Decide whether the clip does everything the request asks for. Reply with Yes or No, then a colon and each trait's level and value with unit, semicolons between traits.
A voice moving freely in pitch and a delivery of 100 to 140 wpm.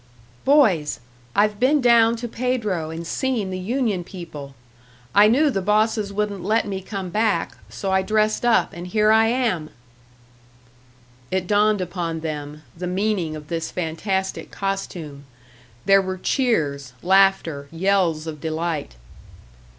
No: average, 4.5 semitones; slow, 135 wpm